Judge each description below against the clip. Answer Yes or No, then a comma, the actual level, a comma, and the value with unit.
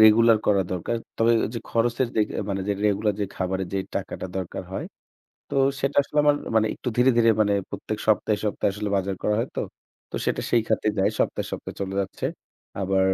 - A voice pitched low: Yes, low, 105 Hz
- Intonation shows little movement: No, average, 3.0 semitones